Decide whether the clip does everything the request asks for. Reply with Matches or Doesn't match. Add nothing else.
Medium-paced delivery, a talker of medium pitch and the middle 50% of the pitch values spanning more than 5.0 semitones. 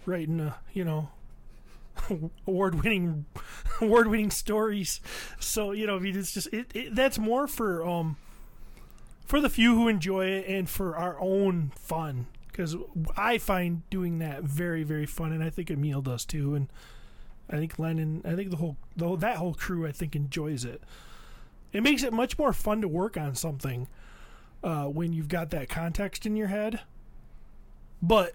Doesn't match